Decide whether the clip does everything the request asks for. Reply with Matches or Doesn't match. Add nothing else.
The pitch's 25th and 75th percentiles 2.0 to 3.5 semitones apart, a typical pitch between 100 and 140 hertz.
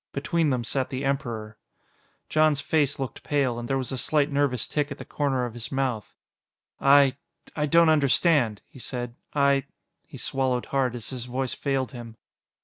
Matches